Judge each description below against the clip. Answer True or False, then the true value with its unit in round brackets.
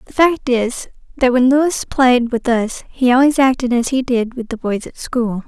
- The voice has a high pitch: True (250 Hz)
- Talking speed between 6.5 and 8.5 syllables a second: False (4.5 syllables/s)